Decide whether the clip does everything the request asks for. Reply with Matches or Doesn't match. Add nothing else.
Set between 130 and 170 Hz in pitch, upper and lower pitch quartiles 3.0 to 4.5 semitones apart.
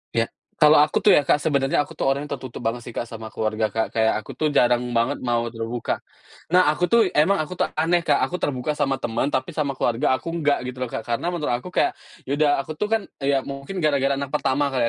Matches